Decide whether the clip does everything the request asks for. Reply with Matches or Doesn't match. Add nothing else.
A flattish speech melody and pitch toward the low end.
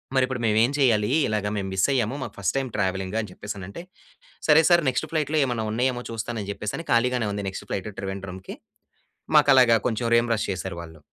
Doesn't match